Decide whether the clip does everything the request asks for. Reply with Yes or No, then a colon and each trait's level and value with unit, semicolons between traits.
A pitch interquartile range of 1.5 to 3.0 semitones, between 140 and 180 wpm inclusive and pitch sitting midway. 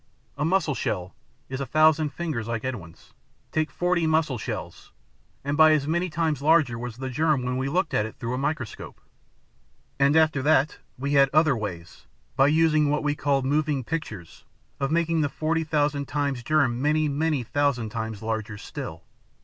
No: average, 4.0 semitones; average, 175 wpm; medium, 145 Hz